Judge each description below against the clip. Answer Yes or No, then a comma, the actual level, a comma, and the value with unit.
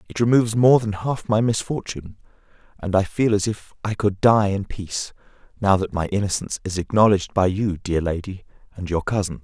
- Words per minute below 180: No, average, 190 wpm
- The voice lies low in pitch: Yes, low, 100 Hz